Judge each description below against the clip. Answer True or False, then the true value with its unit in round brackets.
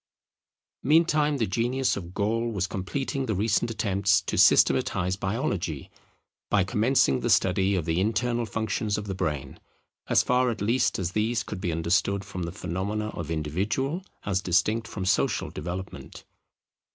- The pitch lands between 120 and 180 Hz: False (100 Hz)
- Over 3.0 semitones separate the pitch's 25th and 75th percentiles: True (4.1 semitones)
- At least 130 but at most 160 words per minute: True (150 wpm)